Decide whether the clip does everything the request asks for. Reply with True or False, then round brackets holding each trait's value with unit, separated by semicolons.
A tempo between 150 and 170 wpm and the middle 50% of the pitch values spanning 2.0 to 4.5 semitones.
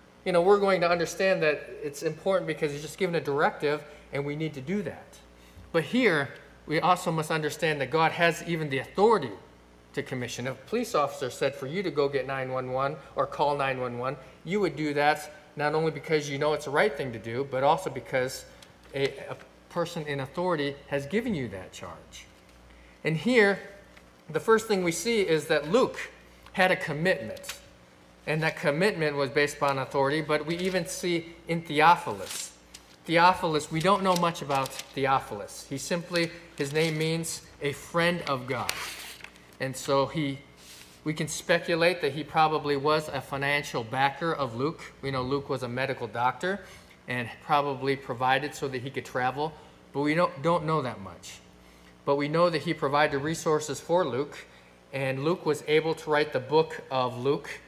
False (180 wpm; 3.8 semitones)